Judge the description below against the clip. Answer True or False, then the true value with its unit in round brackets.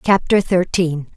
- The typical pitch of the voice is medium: True (175 Hz)